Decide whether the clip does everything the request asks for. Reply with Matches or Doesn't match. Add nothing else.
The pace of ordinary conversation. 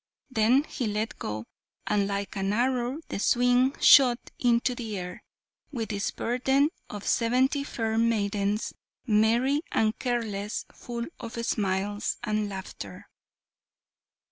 Doesn't match